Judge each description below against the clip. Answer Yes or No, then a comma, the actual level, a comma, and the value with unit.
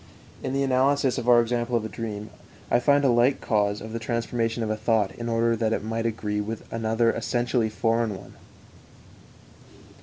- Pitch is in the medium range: No, low, 115 Hz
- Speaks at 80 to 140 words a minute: No, average, 185 wpm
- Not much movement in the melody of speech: Yes, narrow, 1.6 semitones